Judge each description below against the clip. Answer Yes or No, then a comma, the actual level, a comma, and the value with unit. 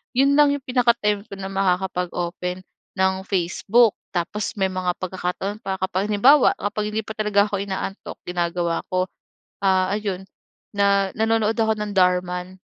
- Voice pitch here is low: No, high, 195 Hz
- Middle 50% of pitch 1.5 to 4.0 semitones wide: Yes, narrow, 2.6 semitones